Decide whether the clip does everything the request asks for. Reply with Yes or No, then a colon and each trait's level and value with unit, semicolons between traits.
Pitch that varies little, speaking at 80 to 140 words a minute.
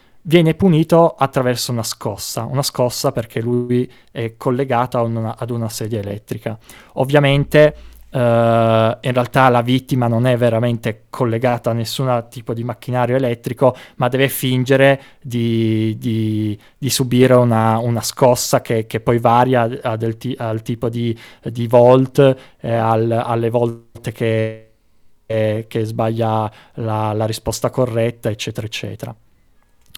Yes: narrow, 2.2 semitones; average, 135 wpm